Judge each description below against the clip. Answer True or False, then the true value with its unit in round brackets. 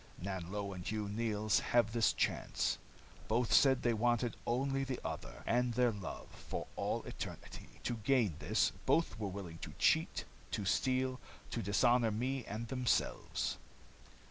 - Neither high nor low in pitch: False (115 Hz)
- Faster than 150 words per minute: False (145 wpm)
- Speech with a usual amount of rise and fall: True (3.3 semitones)